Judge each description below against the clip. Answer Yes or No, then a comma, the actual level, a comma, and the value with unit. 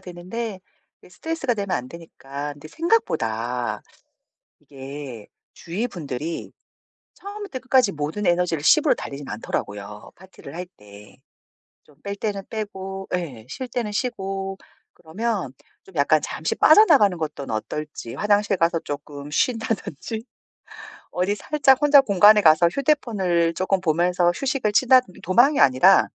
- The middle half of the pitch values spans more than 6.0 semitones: Yes, wide, 7.1 semitones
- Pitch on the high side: No, medium, 180 Hz